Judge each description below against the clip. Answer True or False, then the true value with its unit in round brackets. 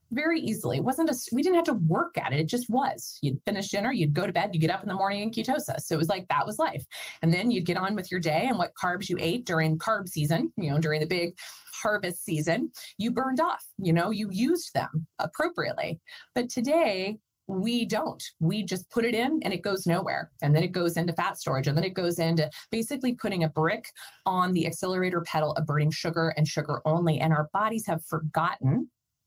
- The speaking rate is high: True (235 wpm)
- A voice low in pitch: False (180 Hz)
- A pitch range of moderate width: False (5.7 semitones)